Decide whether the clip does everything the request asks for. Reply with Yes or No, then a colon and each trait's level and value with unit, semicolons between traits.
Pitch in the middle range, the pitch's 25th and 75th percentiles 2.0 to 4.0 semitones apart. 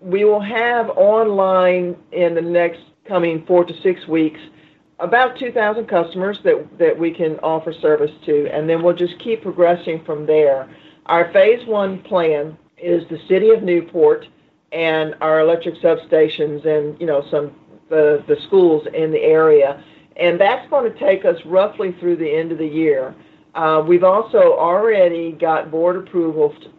No: medium, 175 Hz; average, 4.6 semitones